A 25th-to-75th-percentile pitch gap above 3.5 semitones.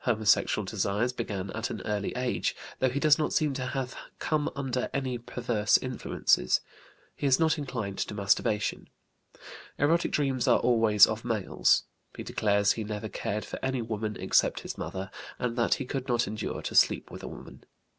Yes: average, 3.9 semitones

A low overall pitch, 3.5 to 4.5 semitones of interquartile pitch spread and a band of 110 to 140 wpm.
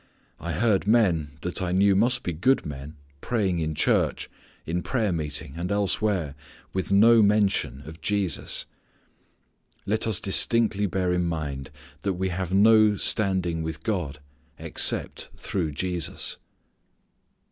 Yes: very low, 95 Hz; average, 4.0 semitones; slow, 135 wpm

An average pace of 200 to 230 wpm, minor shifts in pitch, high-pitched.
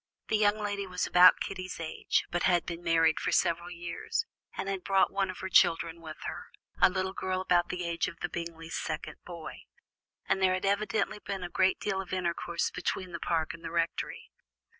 No: fast, 205 wpm; narrow, 2.2 semitones; medium, 180 Hz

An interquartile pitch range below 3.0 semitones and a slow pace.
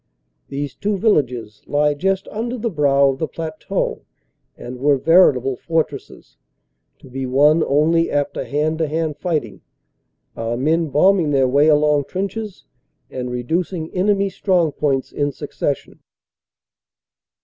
No: average, 3.9 semitones; slow, 130 wpm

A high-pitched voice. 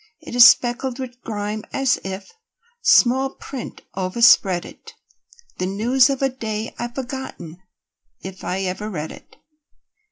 Yes: high, 230 Hz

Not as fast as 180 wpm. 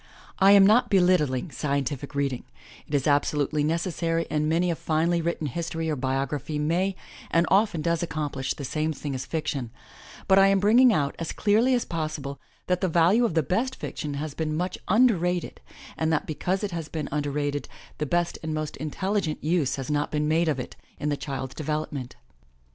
No: average, 195 wpm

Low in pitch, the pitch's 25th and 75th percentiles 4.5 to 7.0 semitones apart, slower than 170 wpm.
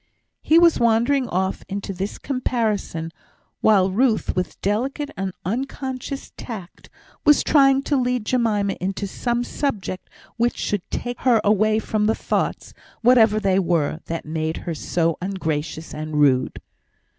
No: high, 210 Hz; average, 5.2 semitones; average, 140 wpm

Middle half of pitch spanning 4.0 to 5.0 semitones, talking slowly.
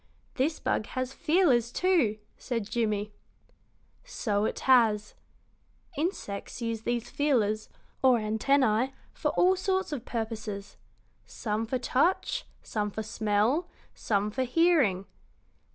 Yes: average, 4.7 semitones; slow, 115 wpm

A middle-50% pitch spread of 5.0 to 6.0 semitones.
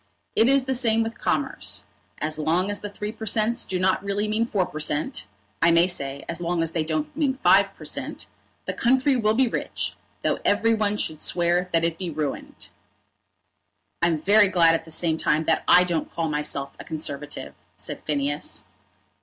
Yes: average, 5.3 semitones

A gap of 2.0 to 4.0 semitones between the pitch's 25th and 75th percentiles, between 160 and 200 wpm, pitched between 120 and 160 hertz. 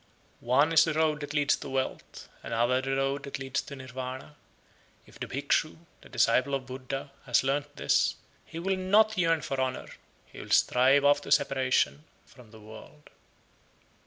Yes: narrow, 2.4 semitones; average, 170 wpm; low, 135 Hz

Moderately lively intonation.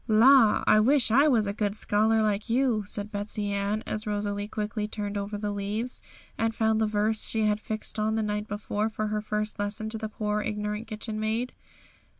No: narrow, 1.0 semitones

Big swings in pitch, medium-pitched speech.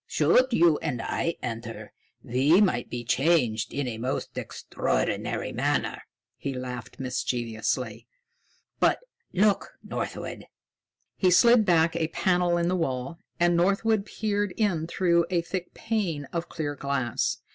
Yes: wide, 6.3 semitones; medium, 165 Hz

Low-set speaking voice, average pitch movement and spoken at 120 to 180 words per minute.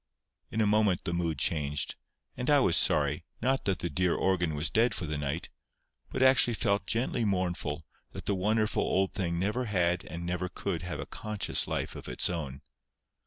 No: very low, 90 Hz; average, 4.1 semitones; average, 190 wpm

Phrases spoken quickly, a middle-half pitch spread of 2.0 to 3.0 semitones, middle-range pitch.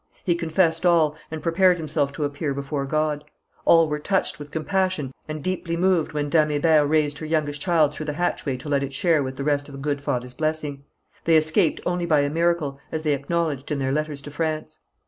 Yes: fast, 210 wpm; narrow, 2.5 semitones; medium, 155 Hz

